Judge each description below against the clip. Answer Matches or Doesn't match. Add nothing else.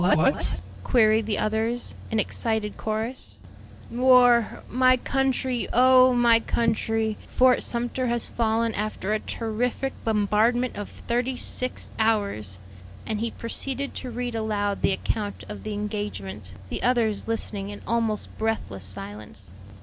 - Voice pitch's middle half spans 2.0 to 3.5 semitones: Matches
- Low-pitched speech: Doesn't match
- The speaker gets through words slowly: Matches